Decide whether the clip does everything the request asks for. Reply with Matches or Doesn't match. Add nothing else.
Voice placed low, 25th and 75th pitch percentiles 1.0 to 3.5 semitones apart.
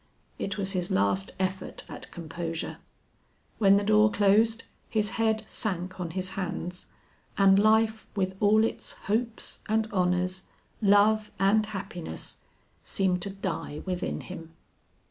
Doesn't match